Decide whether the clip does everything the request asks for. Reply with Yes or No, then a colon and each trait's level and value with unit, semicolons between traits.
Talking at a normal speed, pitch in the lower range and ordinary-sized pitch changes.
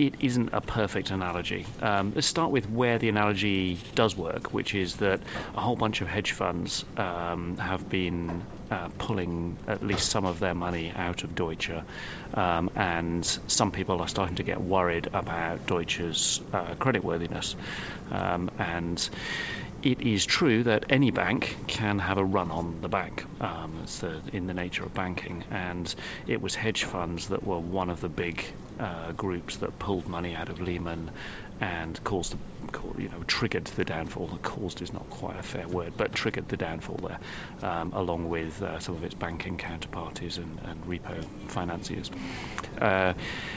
Yes: average, 175 wpm; very low, 90 Hz; average, 3.2 semitones